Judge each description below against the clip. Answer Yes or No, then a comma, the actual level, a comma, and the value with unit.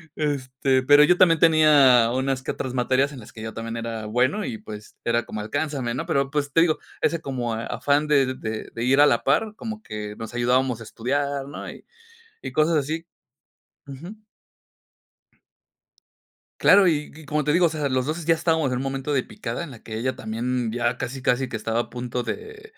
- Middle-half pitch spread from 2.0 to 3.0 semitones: No, average, 4.1 semitones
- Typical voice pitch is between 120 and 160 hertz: Yes, low, 135 Hz